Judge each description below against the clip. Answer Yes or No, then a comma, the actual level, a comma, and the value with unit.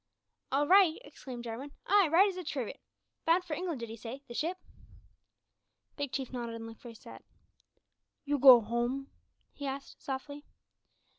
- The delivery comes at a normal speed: Yes, average, 160 wpm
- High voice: Yes, very high, 275 Hz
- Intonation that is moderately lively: Yes, average, 4.8 semitones